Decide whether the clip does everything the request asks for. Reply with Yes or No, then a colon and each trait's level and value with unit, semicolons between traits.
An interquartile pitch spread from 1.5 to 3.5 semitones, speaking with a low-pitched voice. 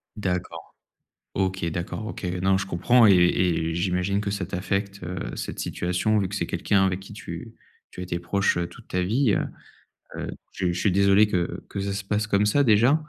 Yes: narrow, 2.4 semitones; very low, 95 Hz